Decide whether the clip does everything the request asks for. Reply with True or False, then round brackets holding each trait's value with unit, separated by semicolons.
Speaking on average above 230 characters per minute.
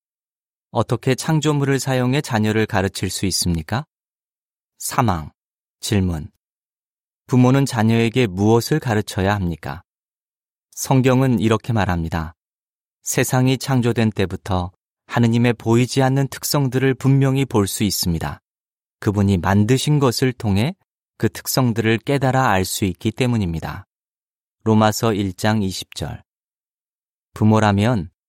True (250 characters per minute)